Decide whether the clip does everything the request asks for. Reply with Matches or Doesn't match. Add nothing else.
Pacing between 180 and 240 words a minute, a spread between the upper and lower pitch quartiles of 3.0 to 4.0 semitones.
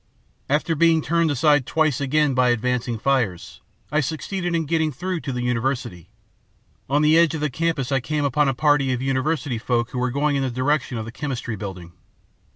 Matches